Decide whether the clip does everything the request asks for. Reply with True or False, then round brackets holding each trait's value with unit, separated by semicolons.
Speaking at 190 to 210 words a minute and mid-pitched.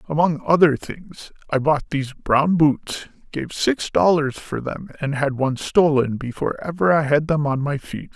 False (170 wpm; 150 Hz)